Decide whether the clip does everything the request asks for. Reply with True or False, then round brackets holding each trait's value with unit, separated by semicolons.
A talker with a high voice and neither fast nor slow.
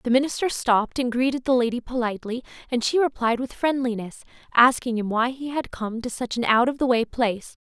False (245 Hz; 210 wpm)